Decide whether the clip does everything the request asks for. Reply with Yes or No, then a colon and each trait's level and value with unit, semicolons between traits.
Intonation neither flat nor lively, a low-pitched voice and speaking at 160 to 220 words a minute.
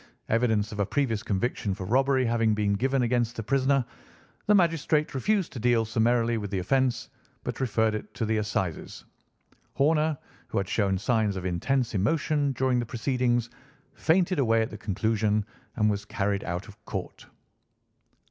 Yes: average, 4.1 semitones; low, 115 Hz; average, 165 wpm